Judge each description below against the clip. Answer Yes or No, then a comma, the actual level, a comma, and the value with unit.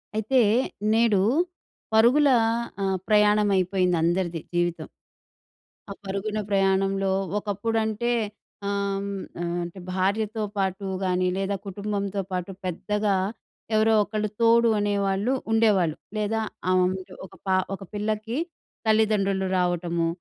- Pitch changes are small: Yes, narrow, 2.3 semitones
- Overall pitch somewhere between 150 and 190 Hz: No, high, 200 Hz